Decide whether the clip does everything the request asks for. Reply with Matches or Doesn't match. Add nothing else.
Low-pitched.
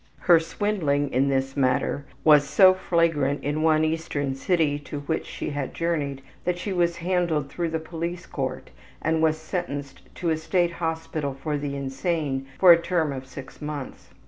Doesn't match